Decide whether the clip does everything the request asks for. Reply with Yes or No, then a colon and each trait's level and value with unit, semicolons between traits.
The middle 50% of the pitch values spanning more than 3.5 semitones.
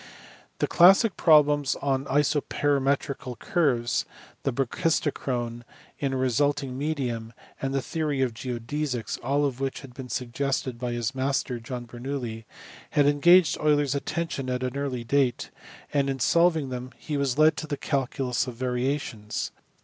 No: average, 2.7 semitones